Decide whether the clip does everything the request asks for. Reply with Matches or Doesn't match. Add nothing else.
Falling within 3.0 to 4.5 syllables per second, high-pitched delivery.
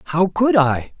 Doesn't match